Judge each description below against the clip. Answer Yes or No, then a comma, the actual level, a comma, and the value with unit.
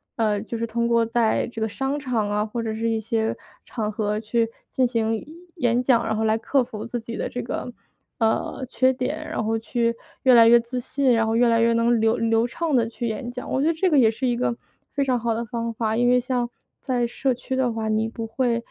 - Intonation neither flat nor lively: No, narrow, 1.8 semitones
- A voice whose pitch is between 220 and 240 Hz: Yes, high, 235 Hz